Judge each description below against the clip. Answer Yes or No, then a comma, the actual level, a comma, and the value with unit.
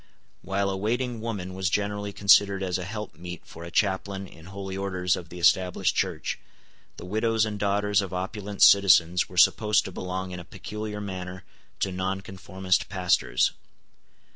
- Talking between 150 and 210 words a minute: Yes, average, 165 wpm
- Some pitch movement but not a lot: No, narrow, 2.0 semitones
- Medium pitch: No, very low, 95 Hz